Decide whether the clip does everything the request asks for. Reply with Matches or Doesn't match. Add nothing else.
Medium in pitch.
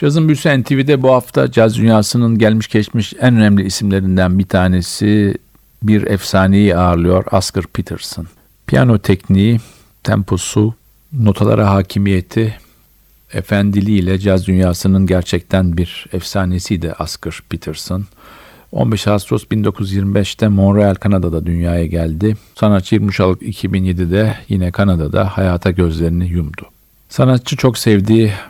Doesn't match